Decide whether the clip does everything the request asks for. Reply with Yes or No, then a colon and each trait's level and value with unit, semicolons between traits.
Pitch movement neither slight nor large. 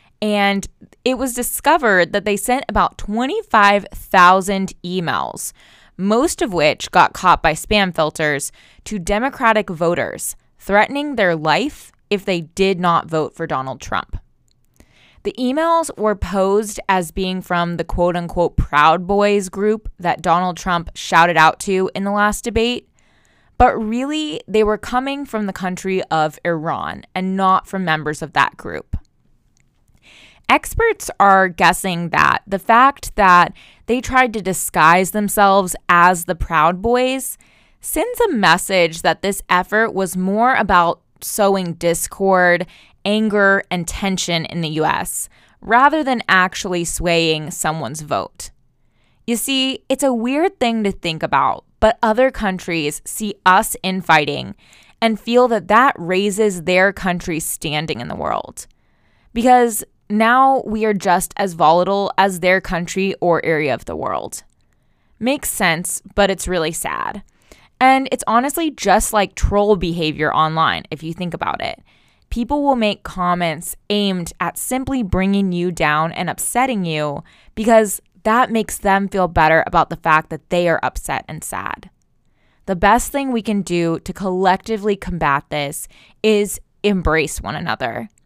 Yes: average, 4.3 semitones